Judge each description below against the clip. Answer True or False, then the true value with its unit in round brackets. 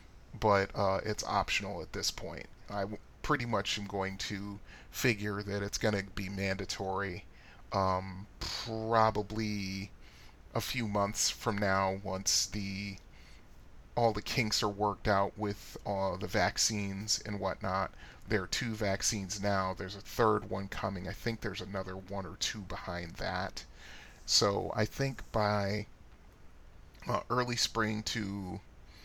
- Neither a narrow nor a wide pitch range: False (2.0 semitones)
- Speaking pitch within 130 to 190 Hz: False (100 Hz)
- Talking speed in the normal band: True (145 wpm)